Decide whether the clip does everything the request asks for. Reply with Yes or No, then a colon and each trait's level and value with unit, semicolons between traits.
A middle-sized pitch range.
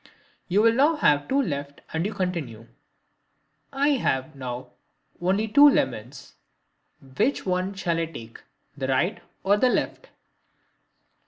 No: wide, 8.2 semitones